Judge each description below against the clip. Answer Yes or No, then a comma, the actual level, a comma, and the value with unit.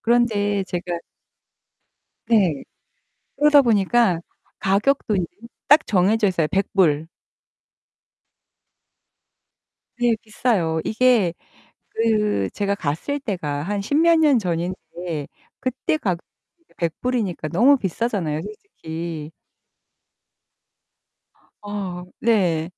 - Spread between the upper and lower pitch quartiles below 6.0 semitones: Yes, wide, 5.6 semitones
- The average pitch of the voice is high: Yes, high, 200 Hz